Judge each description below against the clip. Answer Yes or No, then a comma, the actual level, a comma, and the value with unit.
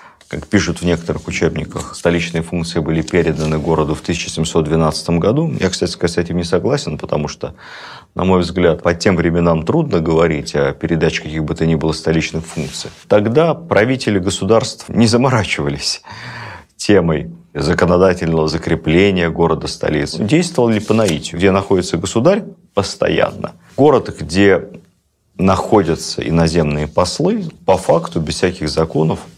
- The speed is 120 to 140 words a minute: Yes, average, 135 wpm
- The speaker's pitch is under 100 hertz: Yes, very low, 85 Hz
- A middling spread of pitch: Yes, average, 3.8 semitones